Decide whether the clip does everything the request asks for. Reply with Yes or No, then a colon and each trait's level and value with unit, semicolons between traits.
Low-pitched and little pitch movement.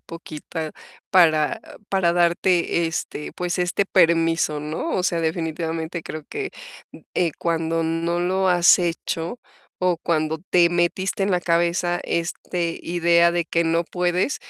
No: medium, 170 Hz; narrow, 1.4 semitones